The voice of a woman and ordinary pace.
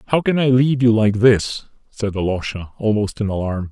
No: male; average, 195 wpm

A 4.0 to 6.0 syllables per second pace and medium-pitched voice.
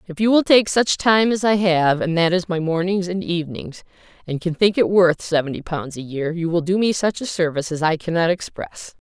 Yes: 5.3 syllables/s; medium, 175 Hz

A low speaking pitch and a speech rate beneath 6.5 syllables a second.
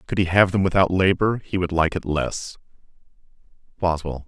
Yes: very low, 90 Hz; 5.2 syllables/s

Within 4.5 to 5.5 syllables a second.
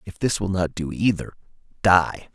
Yes: 4.7 syllables/s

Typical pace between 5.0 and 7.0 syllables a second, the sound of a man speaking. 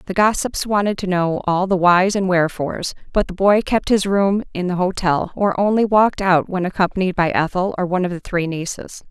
No: 5.5 syllables/s; female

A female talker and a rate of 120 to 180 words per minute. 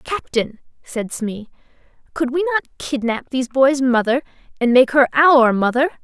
Yes: female; average, 150 wpm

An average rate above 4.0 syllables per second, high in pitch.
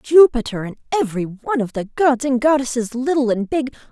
Yes: 5.9 syllables/s; very high, 255 Hz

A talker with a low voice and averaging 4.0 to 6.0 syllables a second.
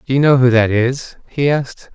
Yes: low, 130 Hz; 5.2 syllables/s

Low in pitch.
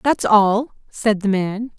No: high, 215 Hz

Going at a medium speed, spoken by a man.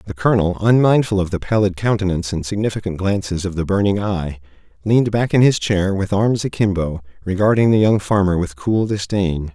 Yes: average, 180 wpm; male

